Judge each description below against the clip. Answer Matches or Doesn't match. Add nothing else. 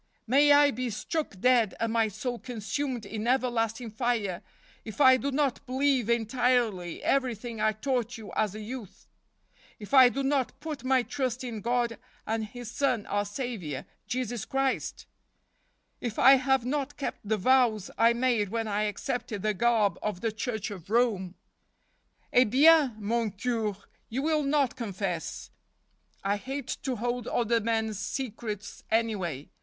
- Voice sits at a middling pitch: Doesn't match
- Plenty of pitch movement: Doesn't match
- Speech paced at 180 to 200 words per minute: Doesn't match